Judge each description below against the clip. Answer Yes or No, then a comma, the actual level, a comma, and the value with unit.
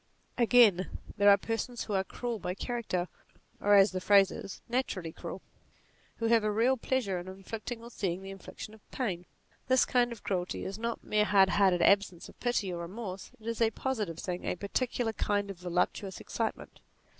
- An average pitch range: Yes, average, 3.7 semitones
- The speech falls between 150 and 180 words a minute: No, average, 190 wpm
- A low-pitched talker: No, high, 205 Hz